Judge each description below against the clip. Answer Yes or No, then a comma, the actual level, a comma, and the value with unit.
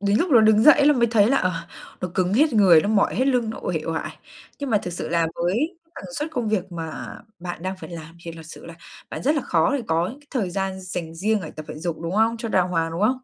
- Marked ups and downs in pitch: Yes, wide, 5.7 semitones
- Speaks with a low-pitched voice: No, high, 195 Hz